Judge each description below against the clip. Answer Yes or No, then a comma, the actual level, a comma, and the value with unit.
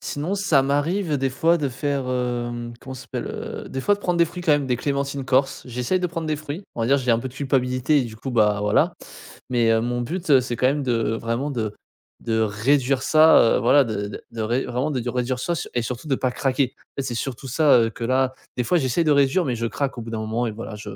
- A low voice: Yes, low, 130 Hz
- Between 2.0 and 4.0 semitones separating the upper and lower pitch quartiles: Yes, average, 3.3 semitones